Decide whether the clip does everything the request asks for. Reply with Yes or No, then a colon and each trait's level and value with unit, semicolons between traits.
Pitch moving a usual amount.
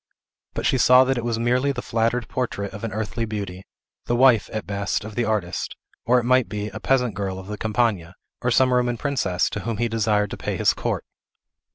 Yes: average, 3.2 semitones